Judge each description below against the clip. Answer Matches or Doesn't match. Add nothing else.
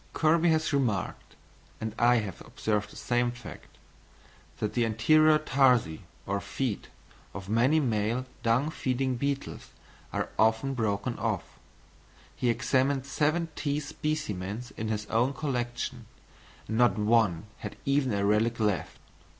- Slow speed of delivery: Matches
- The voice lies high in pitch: Doesn't match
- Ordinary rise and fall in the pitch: Matches